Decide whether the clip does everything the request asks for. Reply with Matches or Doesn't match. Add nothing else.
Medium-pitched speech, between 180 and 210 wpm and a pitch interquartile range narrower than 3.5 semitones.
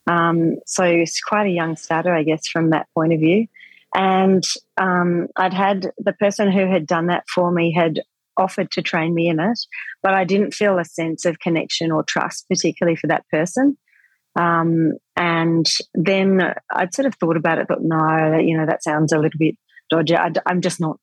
Matches